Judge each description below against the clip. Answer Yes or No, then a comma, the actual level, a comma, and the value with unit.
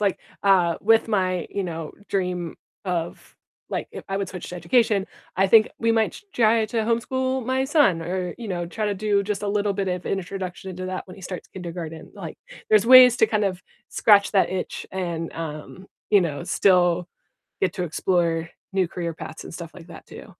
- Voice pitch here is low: No, high, 190 Hz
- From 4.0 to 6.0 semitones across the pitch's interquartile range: No, average, 3.2 semitones